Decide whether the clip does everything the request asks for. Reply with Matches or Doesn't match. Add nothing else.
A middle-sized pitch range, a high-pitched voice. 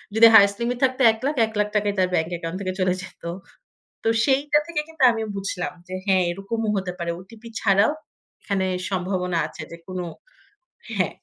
Matches